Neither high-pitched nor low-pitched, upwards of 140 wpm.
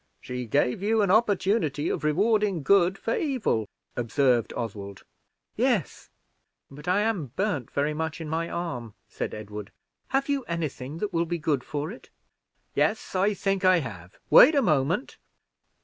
Yes: medium, 165 Hz; average, 160 wpm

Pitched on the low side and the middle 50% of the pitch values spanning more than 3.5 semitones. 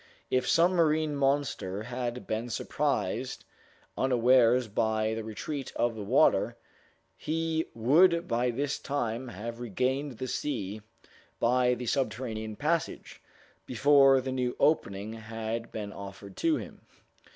Yes: low, 125 Hz; average, 4.1 semitones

